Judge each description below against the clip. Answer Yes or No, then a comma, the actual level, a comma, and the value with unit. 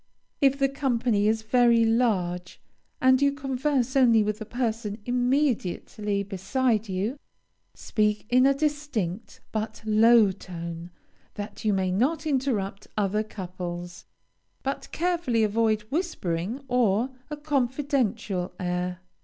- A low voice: No, high, 225 Hz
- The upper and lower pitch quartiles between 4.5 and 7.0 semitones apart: Yes, average, 5.0 semitones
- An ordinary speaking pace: No, slow, 120 wpm